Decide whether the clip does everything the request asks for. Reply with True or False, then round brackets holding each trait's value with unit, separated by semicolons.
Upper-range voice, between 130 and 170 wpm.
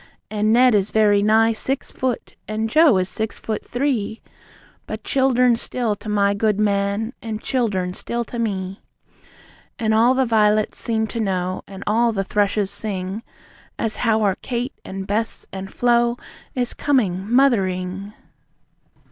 True (215 Hz; 150 wpm)